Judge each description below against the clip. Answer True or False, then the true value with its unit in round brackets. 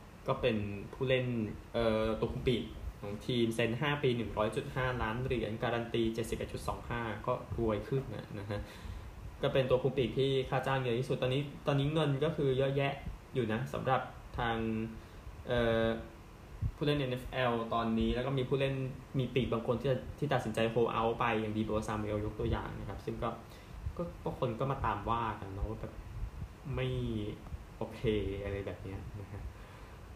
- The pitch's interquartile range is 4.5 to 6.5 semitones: False (3.3 semitones)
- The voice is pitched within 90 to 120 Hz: True (115 Hz)